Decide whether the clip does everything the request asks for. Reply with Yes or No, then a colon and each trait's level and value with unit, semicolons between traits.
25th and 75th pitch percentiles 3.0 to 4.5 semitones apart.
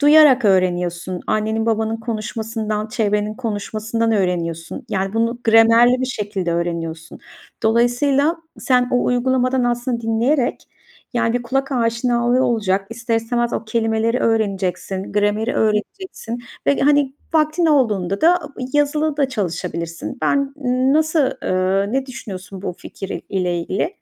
Yes: average, 4.2 semitones